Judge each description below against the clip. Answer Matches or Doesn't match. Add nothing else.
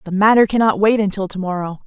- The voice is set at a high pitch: Matches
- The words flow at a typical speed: Doesn't match